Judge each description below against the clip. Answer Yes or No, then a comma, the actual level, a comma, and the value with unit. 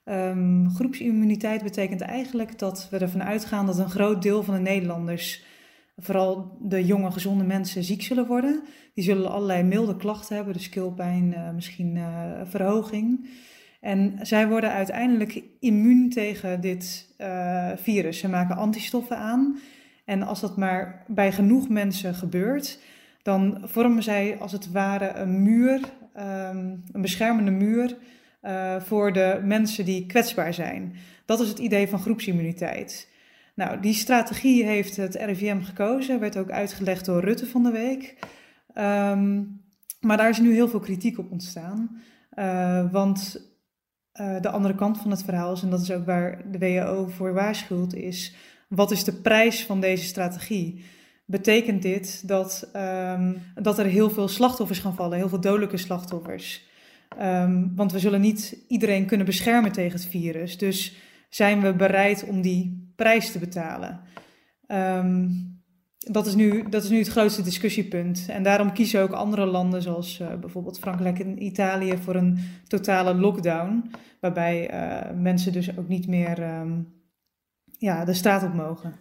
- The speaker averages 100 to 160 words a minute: Yes, average, 155 wpm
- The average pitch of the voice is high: Yes, high, 195 Hz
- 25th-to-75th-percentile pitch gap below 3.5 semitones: Yes, average, 2.9 semitones